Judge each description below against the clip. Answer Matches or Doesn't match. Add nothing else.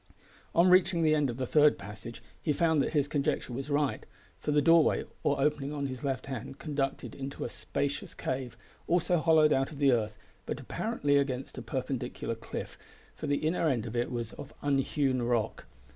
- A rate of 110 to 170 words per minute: Doesn't match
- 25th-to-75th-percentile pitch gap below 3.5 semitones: Matches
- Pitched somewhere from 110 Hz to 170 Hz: Matches